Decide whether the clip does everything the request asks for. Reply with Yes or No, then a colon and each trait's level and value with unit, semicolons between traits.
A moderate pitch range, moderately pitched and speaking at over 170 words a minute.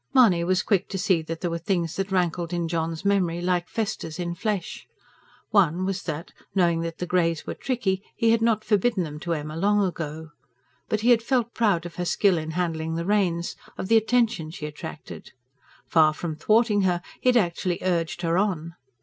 Yes: average, 3.6 semitones; medium, 180 Hz; average, 195 wpm